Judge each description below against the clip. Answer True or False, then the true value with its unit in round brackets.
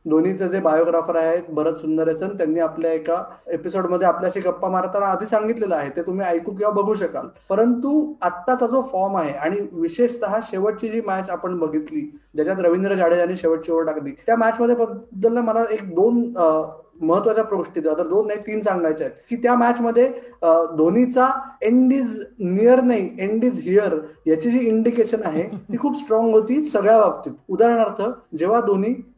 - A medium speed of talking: False (165 wpm)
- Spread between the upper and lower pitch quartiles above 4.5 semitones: True (5.4 semitones)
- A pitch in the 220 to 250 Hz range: False (205 Hz)